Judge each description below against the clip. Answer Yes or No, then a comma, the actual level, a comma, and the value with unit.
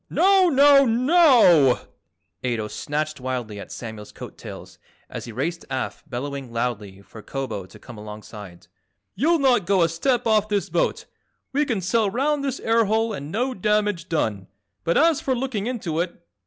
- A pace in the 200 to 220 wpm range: No, average, 170 wpm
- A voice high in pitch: No, medium, 175 Hz